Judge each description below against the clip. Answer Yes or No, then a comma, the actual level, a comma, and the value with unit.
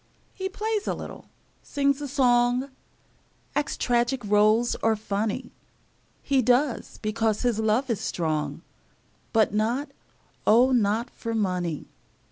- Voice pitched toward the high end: Yes, high, 235 Hz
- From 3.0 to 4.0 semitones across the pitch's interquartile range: Yes, average, 3.7 semitones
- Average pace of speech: No, slow, 120 wpm